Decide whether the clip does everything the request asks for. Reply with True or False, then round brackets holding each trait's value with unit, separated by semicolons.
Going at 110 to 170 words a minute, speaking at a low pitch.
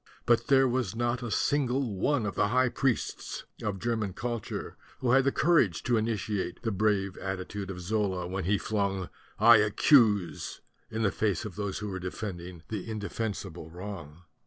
False (180 wpm; 105 Hz)